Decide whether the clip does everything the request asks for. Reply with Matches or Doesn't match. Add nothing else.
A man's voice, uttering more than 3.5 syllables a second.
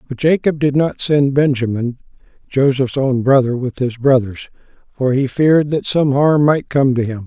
Matches